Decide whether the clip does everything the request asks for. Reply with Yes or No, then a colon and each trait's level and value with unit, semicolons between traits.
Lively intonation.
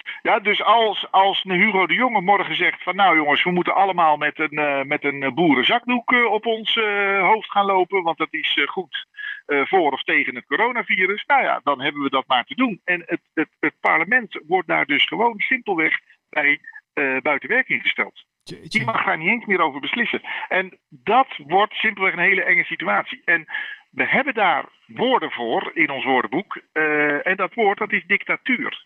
Yes: wide, 6.0 semitones